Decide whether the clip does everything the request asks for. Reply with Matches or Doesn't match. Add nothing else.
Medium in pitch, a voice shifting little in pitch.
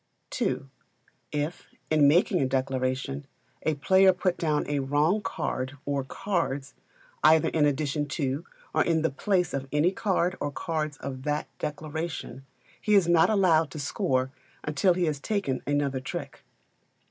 Doesn't match